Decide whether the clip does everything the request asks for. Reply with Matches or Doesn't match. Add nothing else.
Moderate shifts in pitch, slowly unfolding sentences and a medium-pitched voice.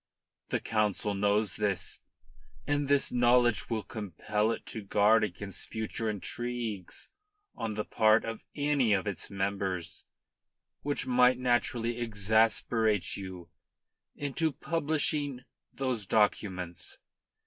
Doesn't match